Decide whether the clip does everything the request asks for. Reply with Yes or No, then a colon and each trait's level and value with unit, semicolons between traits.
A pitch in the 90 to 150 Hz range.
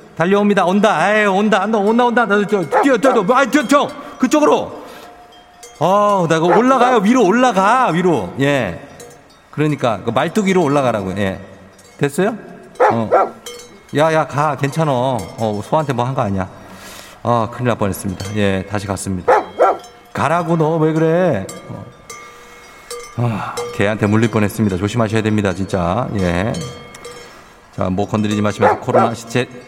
Yes: medium, 140 Hz